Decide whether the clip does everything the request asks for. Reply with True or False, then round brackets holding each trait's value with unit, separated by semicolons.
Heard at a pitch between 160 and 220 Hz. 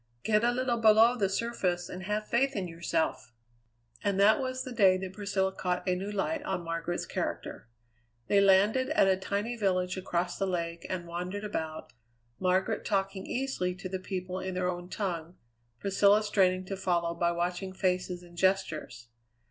True (190 Hz)